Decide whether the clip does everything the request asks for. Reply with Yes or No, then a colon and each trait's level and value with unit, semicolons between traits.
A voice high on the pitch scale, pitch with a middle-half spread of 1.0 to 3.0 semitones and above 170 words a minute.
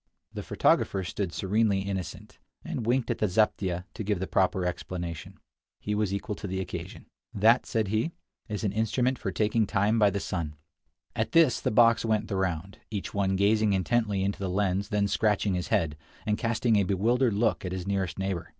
No: low, 100 Hz; narrow, 2.5 semitones; average, 195 wpm